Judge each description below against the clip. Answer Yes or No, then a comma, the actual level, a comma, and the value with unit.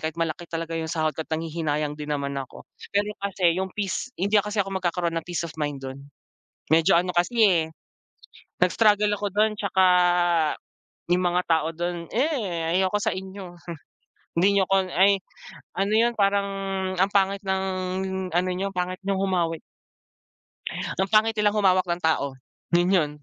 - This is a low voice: No, medium, 180 Hz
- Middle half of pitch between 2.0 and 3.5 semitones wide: Yes, average, 3.2 semitones